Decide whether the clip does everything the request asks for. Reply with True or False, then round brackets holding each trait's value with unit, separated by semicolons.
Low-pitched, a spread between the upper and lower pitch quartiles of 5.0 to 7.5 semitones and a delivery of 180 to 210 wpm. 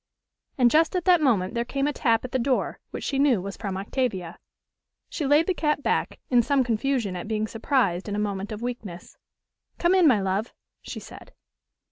False (240 Hz; 5.6 semitones; 200 wpm)